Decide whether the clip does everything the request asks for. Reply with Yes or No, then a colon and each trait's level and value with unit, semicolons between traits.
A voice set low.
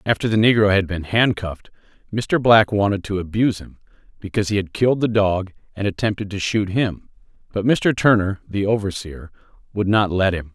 Yes: low, 100 Hz